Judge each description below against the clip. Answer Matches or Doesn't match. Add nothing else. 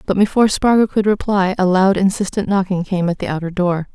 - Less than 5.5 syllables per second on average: Doesn't match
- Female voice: Matches